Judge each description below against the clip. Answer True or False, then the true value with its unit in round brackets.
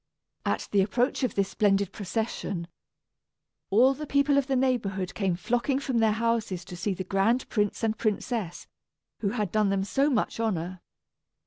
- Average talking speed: True (165 wpm)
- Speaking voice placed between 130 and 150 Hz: False (215 Hz)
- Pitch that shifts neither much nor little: True (4.0 semitones)